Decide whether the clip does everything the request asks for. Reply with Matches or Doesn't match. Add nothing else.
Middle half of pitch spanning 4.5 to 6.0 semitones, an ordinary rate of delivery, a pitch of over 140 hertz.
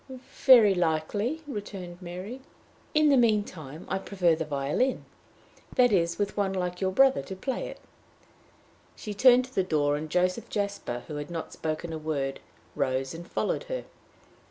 Matches